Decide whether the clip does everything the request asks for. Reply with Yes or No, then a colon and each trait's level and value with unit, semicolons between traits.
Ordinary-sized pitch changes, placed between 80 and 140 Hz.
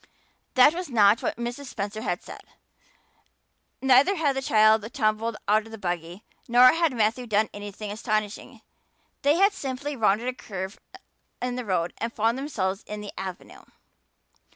No: average, 3.8 semitones; high, 225 Hz